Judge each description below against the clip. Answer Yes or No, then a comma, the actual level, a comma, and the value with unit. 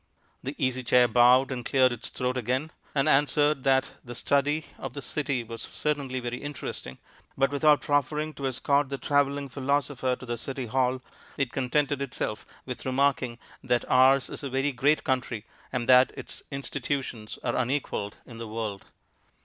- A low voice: Yes, low, 130 Hz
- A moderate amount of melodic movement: No, narrow, 2.3 semitones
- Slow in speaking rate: No, average, 165 wpm